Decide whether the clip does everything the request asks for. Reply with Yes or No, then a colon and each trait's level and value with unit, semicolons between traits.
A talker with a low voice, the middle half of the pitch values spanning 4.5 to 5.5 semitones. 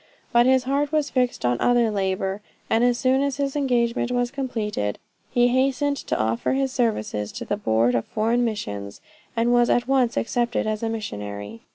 No: high, 240 Hz; average, 5.1 semitones